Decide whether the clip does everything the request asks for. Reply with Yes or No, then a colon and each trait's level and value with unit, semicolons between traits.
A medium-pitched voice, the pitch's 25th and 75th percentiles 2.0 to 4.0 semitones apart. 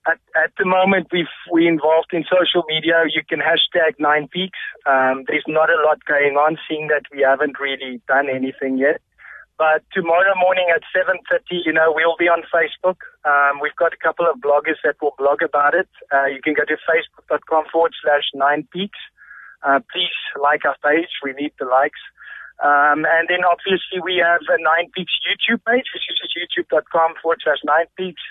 Yes: medium, 165 Hz; average, 3.3 semitones